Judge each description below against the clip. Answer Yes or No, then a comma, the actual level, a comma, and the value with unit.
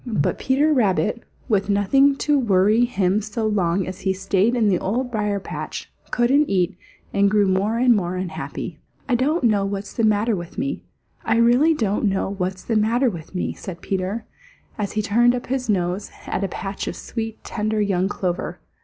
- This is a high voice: Yes, high, 210 Hz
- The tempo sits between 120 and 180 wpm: No, average, 190 wpm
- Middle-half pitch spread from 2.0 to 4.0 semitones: Yes, average, 3.7 semitones